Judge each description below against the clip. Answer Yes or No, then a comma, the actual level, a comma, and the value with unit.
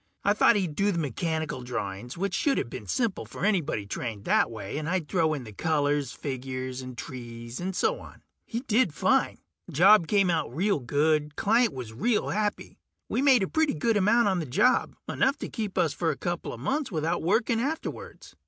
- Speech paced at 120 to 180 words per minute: No, average, 190 wpm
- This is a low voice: No, medium, 160 Hz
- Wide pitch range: Yes, wide, 8.4 semitones